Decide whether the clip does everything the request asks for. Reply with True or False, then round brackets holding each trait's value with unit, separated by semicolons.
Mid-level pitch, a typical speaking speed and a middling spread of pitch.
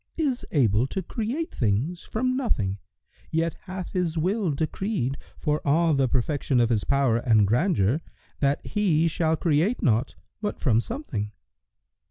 False (155 Hz; 145 wpm; 7.6 semitones)